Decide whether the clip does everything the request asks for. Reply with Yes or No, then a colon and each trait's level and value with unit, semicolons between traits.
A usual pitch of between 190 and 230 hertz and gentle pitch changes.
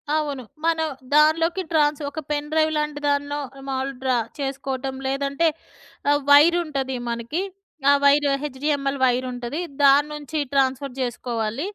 No: very high, 285 Hz; narrow, 2.2 semitones